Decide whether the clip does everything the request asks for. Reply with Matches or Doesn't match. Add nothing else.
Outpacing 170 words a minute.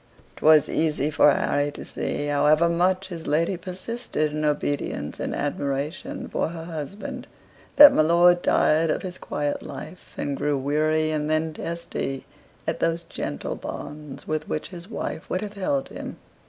Doesn't match